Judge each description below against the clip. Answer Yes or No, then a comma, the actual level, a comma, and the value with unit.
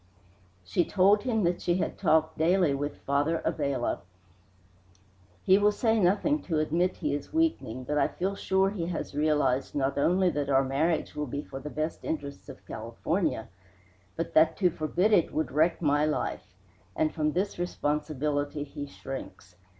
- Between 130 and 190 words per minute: Yes, average, 165 wpm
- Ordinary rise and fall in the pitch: Yes, average, 4.0 semitones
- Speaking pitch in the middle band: Yes, medium, 155 Hz